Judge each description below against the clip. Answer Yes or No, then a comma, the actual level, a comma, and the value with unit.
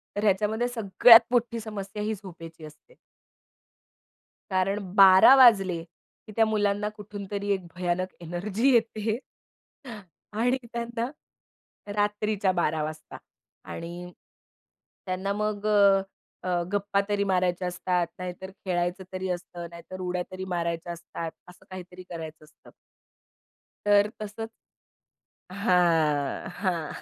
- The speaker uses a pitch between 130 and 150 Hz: No, high, 190 Hz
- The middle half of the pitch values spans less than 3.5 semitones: Yes, average, 3.1 semitones